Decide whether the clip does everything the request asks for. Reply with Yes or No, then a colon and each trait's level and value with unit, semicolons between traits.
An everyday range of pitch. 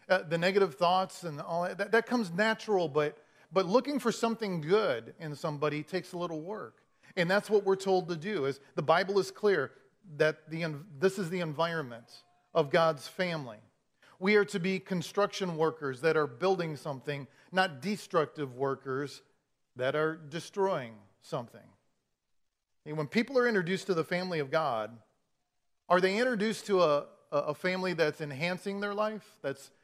Yes: average, 4.6 semitones